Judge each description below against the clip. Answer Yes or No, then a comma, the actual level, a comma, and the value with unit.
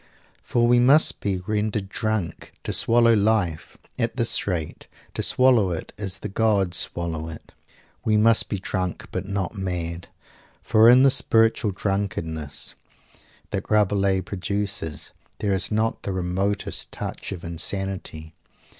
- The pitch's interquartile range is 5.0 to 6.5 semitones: No, average, 3.4 semitones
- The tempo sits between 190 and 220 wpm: No, slow, 135 wpm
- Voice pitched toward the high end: No, low, 100 Hz